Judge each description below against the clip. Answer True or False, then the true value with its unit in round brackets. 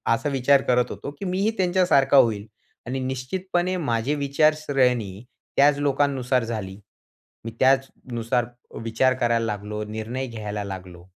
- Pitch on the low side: True (130 Hz)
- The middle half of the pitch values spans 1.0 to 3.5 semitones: False (4.1 semitones)